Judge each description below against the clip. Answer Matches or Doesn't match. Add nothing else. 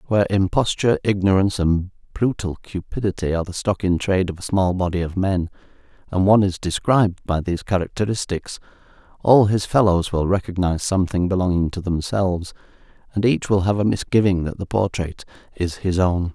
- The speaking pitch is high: Doesn't match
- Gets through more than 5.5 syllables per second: Matches